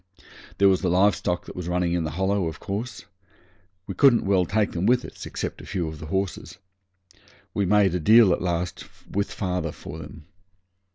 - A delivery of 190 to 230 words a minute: Yes, average, 195 wpm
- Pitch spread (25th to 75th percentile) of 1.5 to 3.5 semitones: Yes, average, 2.8 semitones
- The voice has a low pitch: Yes, very low, 90 Hz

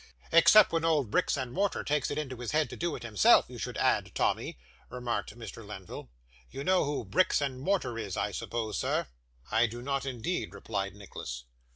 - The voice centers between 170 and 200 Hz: No, low, 125 Hz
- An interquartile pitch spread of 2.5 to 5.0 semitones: No, wide, 5.5 semitones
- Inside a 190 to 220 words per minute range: Yes, average, 195 wpm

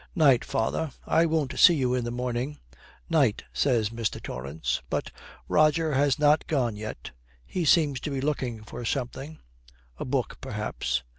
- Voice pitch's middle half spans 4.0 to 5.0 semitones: Yes, average, 4.4 semitones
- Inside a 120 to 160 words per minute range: Yes, average, 155 wpm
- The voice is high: No, low, 135 Hz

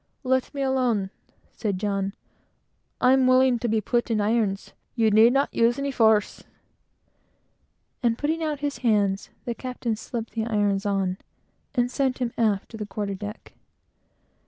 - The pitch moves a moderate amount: Yes, average, 3.7 semitones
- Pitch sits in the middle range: No, high, 230 Hz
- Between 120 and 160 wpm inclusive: Yes, average, 155 wpm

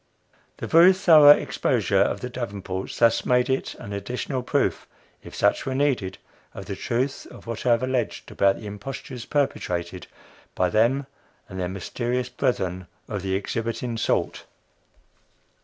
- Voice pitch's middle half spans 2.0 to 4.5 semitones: No, average, 4.9 semitones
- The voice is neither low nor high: No, low, 120 Hz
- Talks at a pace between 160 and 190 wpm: No, average, 150 wpm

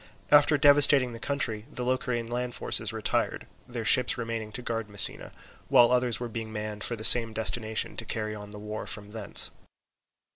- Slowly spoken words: No, average, 180 wpm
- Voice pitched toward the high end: No, low, 115 Hz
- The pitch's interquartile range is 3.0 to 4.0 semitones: No, narrow, 2.5 semitones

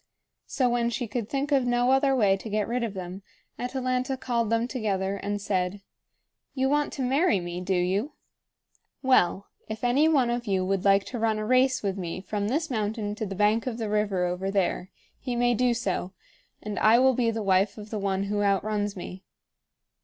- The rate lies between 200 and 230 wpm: Yes, fast, 205 wpm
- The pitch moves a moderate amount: Yes, average, 4.1 semitones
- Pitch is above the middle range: Yes, high, 215 Hz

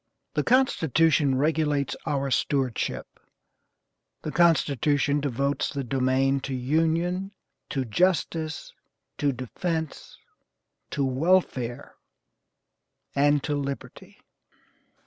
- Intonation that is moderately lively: Yes, average, 3.1 semitones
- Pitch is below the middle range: No, medium, 145 Hz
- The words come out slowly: Yes, slow, 85 wpm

